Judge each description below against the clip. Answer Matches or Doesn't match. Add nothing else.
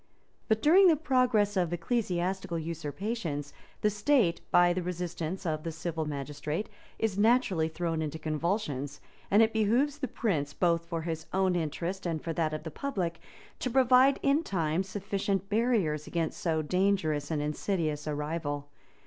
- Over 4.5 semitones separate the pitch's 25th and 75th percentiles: Matches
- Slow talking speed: Doesn't match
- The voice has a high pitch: Doesn't match